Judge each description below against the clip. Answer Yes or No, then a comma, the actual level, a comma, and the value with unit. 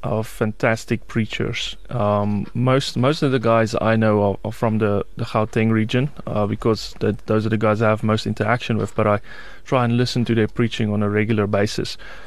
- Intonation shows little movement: Yes, narrow, 2.0 semitones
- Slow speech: No, fast, 205 wpm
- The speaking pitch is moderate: No, low, 110 Hz